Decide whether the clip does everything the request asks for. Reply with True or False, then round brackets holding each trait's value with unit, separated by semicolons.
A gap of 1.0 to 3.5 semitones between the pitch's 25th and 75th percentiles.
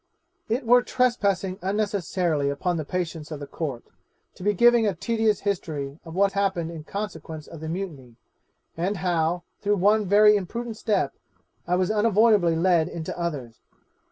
False (4.3 semitones)